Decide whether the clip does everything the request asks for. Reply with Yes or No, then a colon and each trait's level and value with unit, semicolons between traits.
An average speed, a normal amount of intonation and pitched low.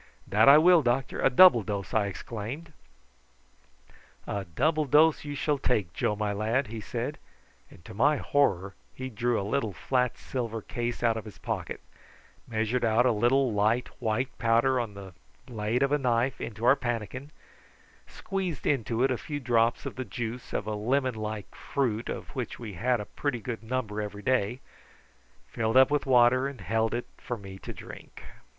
Yes: average, 180 wpm; average, 3.5 semitones; low, 120 Hz